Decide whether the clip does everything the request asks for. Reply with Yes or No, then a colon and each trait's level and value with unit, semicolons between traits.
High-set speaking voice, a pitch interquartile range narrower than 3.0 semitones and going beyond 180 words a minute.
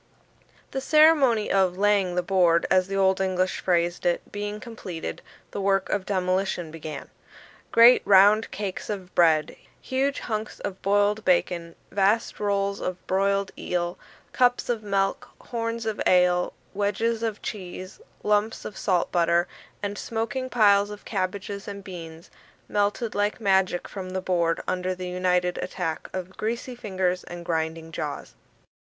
No: high, 195 Hz; narrow, 2.6 semitones; average, 145 wpm